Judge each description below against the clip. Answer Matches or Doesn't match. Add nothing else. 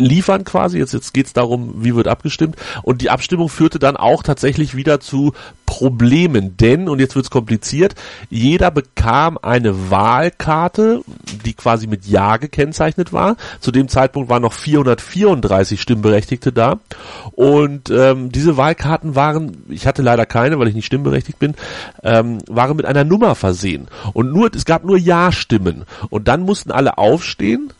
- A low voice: Matches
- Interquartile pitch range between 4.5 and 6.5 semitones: Matches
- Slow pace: Doesn't match